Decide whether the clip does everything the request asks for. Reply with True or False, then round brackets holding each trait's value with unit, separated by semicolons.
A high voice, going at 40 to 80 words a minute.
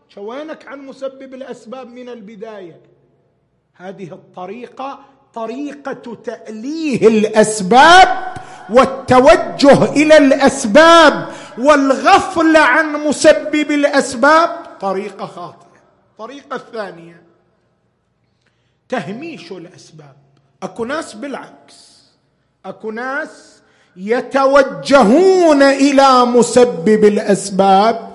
True (250 Hz; 70 wpm)